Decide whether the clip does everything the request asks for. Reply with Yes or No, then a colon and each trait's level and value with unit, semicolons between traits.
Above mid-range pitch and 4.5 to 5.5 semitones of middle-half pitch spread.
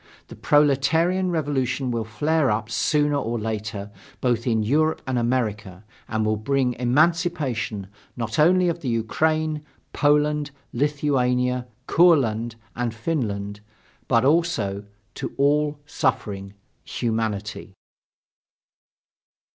No: low, 125 Hz; average, 5.1 semitones